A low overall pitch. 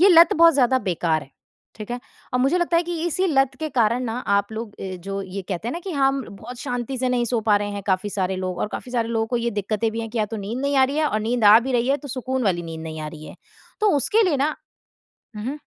No: high, 235 Hz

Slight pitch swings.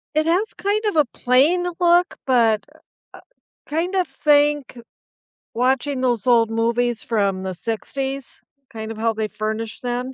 No: average, 5.1 semitones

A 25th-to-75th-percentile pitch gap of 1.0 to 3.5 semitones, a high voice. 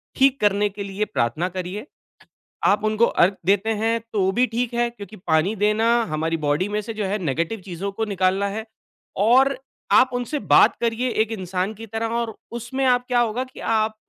Yes: average, 3.2 semitones; high, 215 Hz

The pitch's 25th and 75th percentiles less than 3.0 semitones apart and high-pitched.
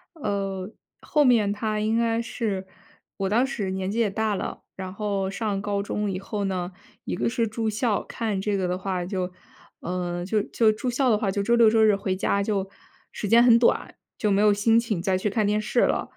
Yes: narrow, 2.6 semitones; high, 205 Hz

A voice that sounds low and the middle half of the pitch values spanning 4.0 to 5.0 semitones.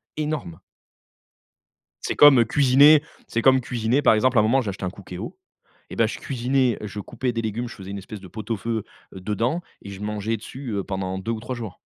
Yes: low, 115 Hz; average, 4.3 semitones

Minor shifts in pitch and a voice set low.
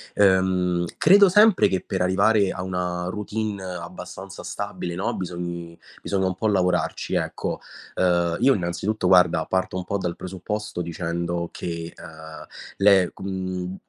Yes: narrow, 2.0 semitones; very low, 90 Hz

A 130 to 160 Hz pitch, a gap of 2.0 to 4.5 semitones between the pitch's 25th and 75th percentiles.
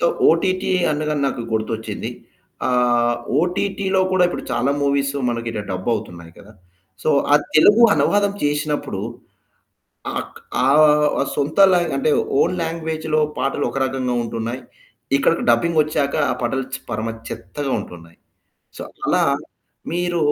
No: medium, 140 Hz; average, 5.3 semitones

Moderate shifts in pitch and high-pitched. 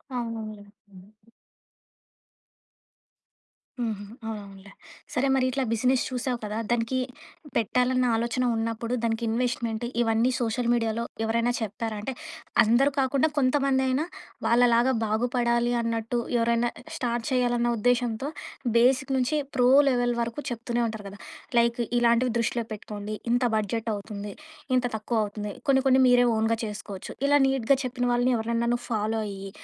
No: narrow, 2.1 semitones; high, 235 Hz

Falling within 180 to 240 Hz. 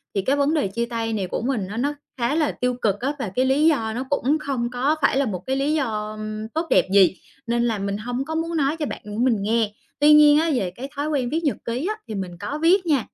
No: very high, 250 Hz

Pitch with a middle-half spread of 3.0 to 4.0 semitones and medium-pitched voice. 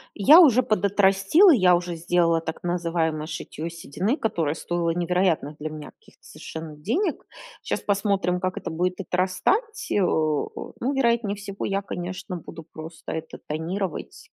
Yes: average, 3.6 semitones; medium, 180 Hz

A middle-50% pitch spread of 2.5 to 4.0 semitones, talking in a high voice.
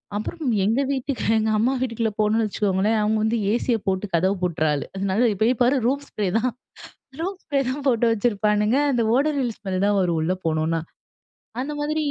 No: average, 4.6 semitones; high, 220 Hz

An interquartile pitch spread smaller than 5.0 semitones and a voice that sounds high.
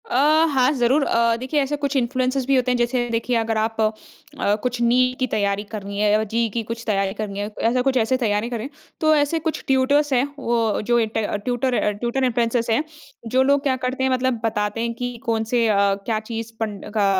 Yes: narrow, 2.6 semitones; high, 235 Hz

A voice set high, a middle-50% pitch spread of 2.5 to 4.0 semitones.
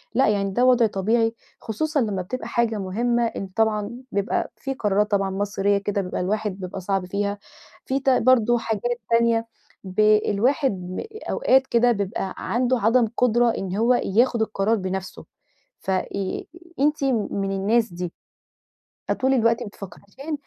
Yes: high, 215 Hz; average, 3.5 semitones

